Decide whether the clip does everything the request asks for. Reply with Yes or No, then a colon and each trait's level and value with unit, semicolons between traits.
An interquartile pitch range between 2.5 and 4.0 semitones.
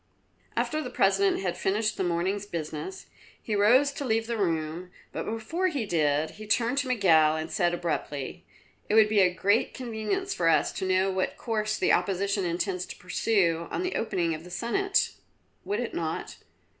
No: average, 4.7 semitones